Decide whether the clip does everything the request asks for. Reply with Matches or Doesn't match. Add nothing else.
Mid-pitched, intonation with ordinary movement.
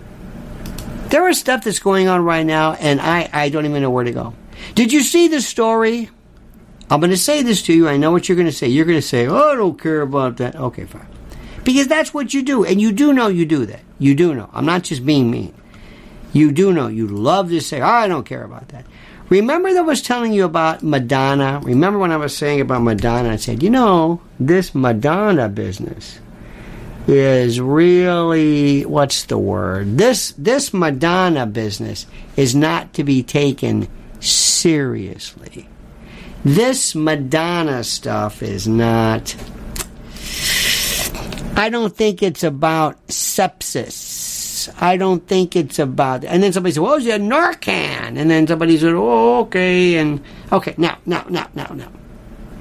Doesn't match